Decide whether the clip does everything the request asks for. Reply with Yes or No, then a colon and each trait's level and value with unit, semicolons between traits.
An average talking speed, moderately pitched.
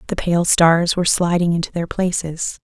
Yes: average, 180 wpm; medium, 170 Hz